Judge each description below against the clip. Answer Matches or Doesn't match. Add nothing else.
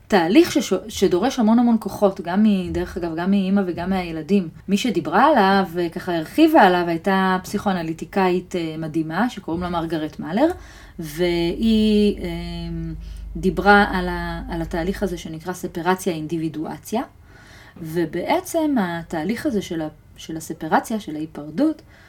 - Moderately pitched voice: Matches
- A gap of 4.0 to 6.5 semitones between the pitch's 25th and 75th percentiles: Doesn't match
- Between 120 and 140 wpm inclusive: Matches